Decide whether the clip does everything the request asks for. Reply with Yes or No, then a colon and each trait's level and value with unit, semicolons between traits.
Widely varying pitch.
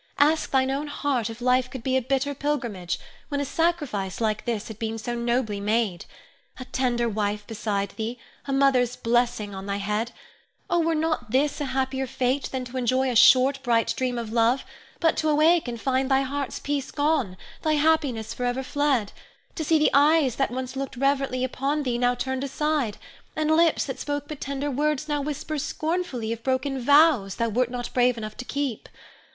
No: average, 3.4 semitones